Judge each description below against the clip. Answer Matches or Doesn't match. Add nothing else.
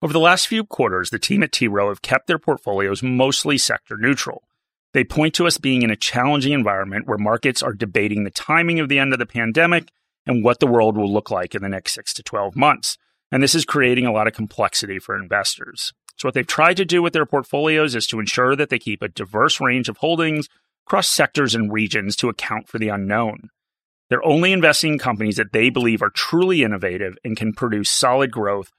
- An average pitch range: Doesn't match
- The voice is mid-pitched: Doesn't match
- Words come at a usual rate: Doesn't match